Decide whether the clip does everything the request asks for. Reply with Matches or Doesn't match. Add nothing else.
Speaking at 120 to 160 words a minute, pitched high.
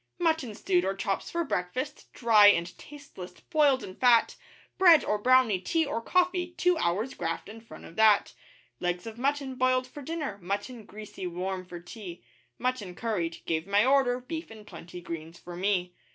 Doesn't match